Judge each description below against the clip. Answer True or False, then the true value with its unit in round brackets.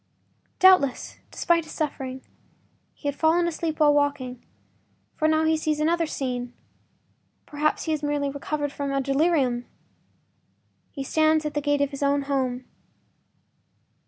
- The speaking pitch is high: True (290 Hz)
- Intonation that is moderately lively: False (2.3 semitones)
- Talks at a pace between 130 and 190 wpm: True (135 wpm)